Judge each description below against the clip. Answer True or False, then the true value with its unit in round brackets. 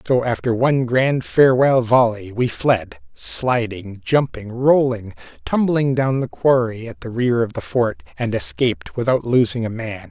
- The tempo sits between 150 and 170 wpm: True (160 wpm)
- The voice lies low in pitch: True (125 Hz)